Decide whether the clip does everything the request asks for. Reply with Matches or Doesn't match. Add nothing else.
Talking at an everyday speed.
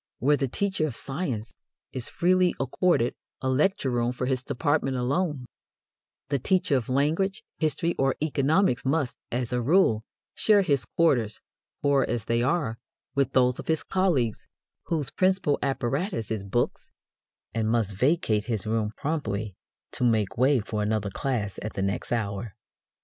Matches